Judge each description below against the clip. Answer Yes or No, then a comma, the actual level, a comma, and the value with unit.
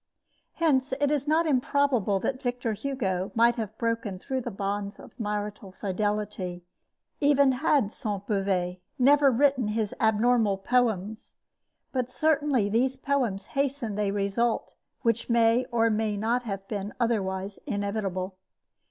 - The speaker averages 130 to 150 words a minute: Yes, slow, 135 wpm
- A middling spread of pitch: Yes, average, 4.3 semitones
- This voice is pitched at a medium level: No, high, 225 Hz